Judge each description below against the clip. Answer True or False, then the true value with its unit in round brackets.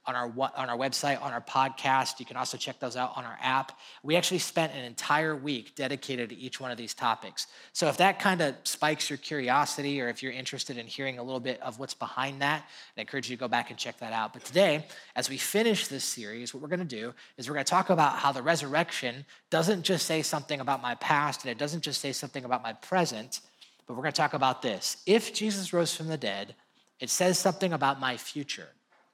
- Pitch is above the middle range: False (140 Hz)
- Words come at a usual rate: False (235 wpm)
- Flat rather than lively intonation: False (3.7 semitones)